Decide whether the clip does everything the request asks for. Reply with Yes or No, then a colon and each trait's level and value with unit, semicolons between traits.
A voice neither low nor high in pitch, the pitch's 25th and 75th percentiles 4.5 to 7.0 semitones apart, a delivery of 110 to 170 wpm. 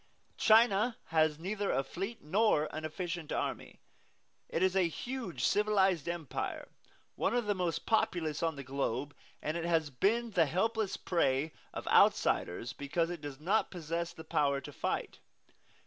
Yes: medium, 170 Hz; average, 4.8 semitones; average, 155 wpm